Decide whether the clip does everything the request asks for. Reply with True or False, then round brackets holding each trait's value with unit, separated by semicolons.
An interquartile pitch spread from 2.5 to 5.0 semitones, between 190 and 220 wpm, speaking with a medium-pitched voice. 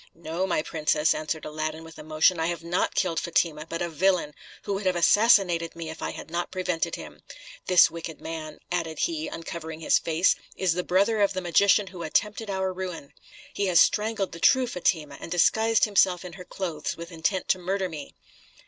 True (2.8 semitones; 195 wpm; 175 Hz)